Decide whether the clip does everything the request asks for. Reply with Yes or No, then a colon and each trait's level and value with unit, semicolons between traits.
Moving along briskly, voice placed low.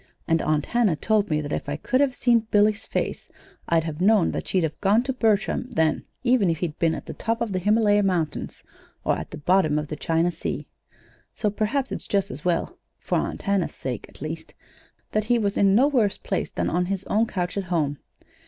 No: fast, 220 wpm; high, 195 Hz